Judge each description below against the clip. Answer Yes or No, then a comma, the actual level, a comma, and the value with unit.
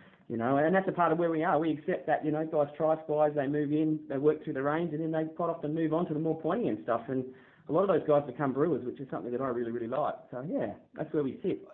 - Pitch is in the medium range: Yes, medium, 150 Hz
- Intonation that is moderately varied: No, narrow, 2.3 semitones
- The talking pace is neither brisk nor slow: No, fast, 310 wpm